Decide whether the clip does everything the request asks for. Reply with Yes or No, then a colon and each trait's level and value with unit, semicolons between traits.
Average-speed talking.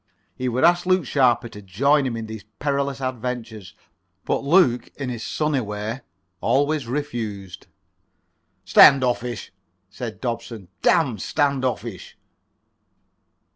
No: slow, 110 wpm